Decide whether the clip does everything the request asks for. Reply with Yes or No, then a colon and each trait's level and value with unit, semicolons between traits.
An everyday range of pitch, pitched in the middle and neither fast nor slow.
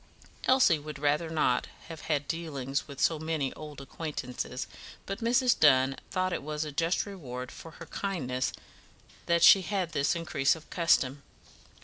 Yes: average, 3.4 semitones; medium, 155 Hz; average, 155 wpm